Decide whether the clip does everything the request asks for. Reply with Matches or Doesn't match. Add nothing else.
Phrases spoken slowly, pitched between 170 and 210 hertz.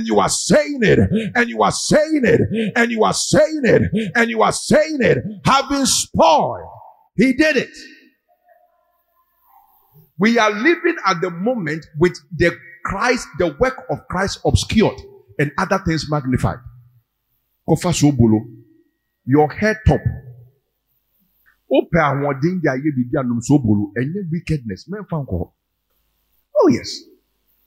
Matches